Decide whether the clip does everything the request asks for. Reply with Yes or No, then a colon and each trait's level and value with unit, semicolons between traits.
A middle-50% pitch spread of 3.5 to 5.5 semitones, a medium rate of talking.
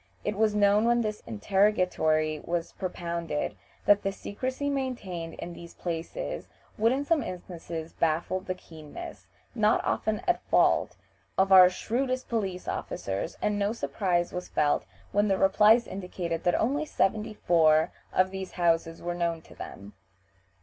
Yes: average, 4.1 semitones; average, 150 wpm